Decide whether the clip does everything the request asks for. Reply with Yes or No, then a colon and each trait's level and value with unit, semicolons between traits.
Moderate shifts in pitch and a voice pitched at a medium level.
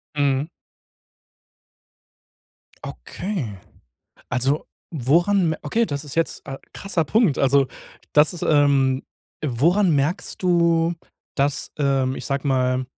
Yes: average, 3.9 semitones; medium, 145 Hz